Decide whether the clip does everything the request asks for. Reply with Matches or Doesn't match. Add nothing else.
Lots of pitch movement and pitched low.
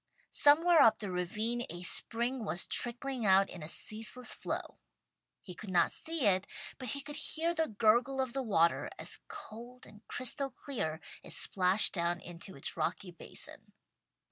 Doesn't match